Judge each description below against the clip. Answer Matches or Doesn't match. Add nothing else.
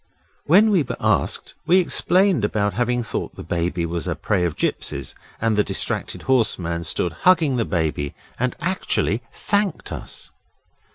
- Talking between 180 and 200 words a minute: Doesn't match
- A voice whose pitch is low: Matches